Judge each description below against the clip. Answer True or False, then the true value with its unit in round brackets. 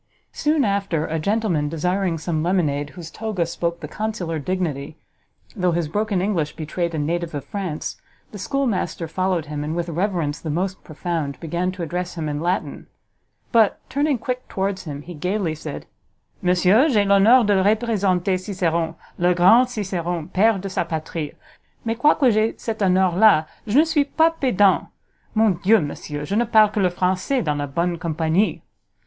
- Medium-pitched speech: True (180 Hz)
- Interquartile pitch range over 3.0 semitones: True (4.4 semitones)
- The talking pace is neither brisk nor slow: True (170 wpm)